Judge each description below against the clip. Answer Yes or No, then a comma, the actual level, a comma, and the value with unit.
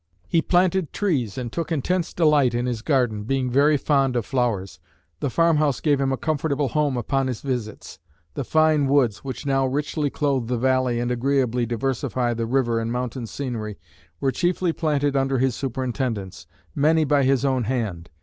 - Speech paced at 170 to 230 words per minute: Yes, average, 175 wpm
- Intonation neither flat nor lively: Yes, average, 3.3 semitones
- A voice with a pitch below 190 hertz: Yes, low, 135 Hz